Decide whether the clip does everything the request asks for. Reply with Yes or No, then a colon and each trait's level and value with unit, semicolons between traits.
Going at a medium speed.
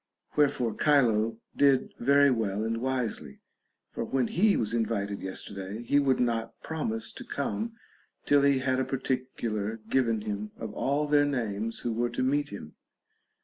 Yes: average, 155 wpm